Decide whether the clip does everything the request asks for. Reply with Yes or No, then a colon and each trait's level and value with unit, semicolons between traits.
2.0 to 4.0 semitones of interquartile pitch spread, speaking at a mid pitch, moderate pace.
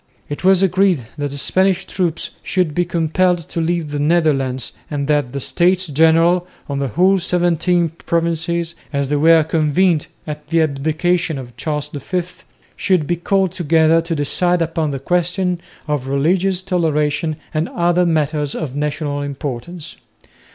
Yes: average, 3.2 semitones; medium, 165 Hz; average, 150 wpm